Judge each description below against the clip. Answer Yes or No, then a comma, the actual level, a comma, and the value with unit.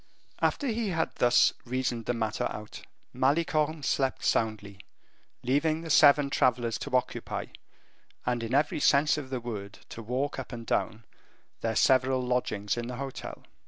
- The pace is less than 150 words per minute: No, average, 155 wpm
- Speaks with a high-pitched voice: No, low, 125 Hz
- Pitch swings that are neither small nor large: Yes, average, 3.7 semitones